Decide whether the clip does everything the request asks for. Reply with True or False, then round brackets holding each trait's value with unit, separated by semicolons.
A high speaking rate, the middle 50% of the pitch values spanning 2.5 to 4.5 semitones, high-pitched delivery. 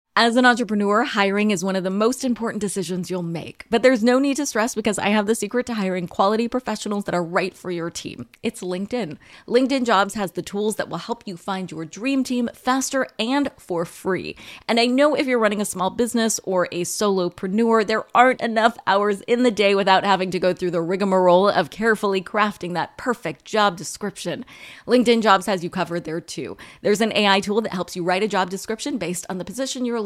True (220 wpm; 4.0 semitones; 205 Hz)